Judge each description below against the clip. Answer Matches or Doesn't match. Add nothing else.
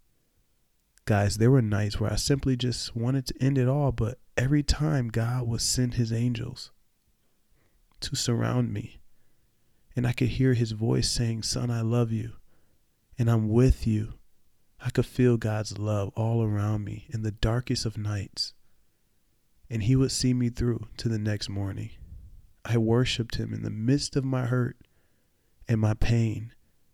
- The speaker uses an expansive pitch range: Doesn't match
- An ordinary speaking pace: Matches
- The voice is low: Matches